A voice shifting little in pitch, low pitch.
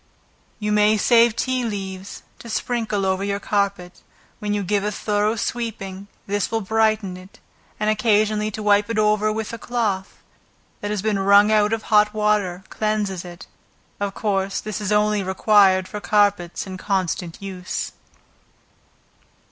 No: narrow, 1.7 semitones; high, 210 Hz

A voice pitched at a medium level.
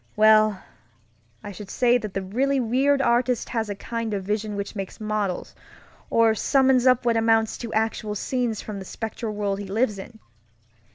No: high, 220 Hz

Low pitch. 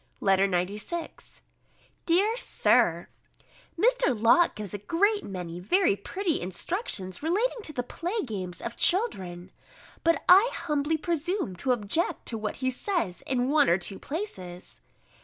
No: very high, 270 Hz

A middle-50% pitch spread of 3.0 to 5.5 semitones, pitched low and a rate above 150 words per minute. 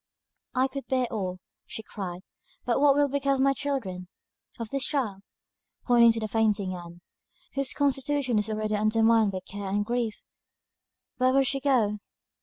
No: average, 4.7 semitones; high, 230 Hz; average, 165 wpm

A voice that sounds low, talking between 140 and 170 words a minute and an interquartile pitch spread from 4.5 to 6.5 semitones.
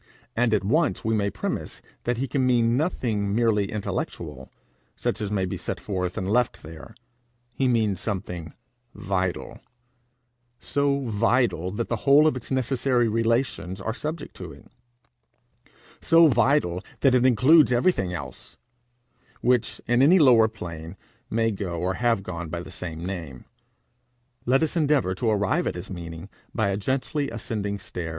Yes: low, 110 Hz; average, 155 wpm; average, 5.3 semitones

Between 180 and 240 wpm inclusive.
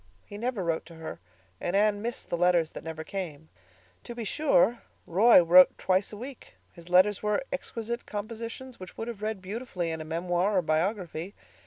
Yes: average, 185 wpm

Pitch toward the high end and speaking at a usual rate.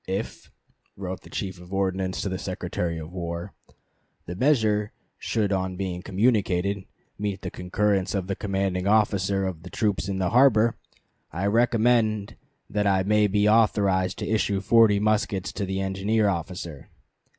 No: low, 100 Hz; average, 155 wpm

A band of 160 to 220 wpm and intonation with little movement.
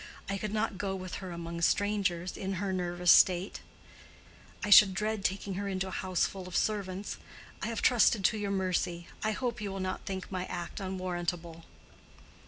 Yes: average, 190 wpm; narrow, 2.1 semitones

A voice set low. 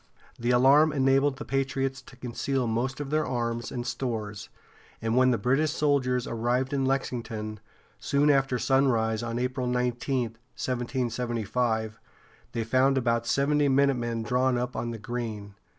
Yes: low, 125 Hz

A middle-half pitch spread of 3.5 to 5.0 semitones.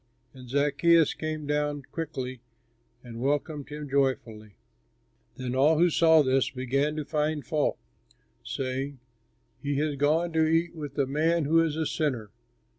No: average, 2.7 semitones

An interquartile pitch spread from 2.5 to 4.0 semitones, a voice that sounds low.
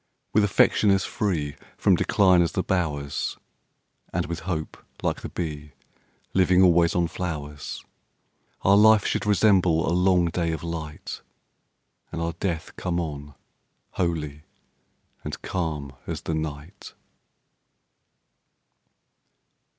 Yes: average, 3.2 semitones; very low, 85 Hz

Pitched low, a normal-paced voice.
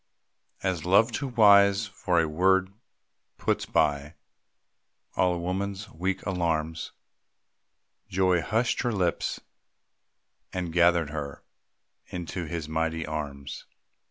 No: very low, 90 Hz; slow, 105 wpm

